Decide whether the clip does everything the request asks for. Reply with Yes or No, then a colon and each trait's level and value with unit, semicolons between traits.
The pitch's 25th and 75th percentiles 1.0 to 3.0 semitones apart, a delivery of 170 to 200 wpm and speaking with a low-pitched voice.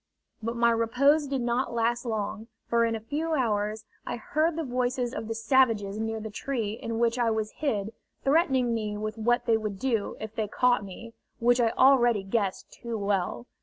No: narrow, 2.5 semitones; average, 195 wpm; high, 230 Hz